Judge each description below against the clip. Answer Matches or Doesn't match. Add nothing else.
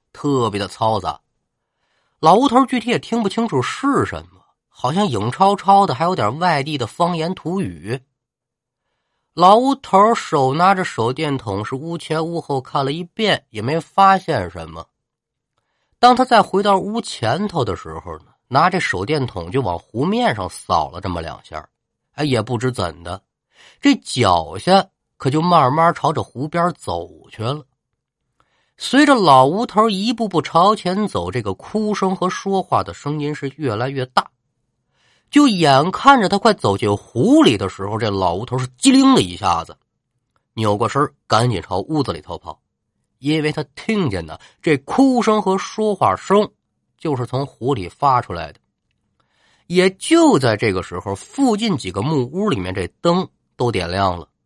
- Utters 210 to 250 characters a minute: Matches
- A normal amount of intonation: Doesn't match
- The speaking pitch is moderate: Matches